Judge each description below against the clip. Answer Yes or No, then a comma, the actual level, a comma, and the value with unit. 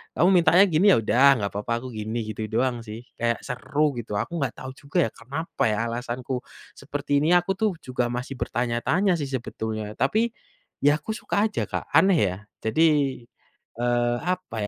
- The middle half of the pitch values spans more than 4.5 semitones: Yes, wide, 5.5 semitones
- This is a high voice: No, low, 130 Hz